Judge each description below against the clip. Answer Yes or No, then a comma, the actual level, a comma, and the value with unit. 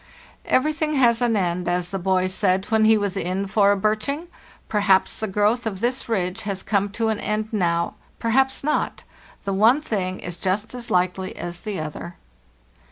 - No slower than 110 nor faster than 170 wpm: No, average, 185 wpm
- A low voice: No, high, 205 Hz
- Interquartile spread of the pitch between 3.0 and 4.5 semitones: Yes, average, 3.4 semitones